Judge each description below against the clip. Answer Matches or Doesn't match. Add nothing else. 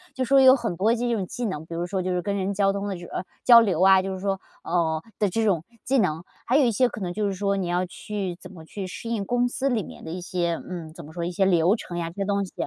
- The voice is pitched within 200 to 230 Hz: Doesn't match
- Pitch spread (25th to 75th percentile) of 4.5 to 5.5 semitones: Doesn't match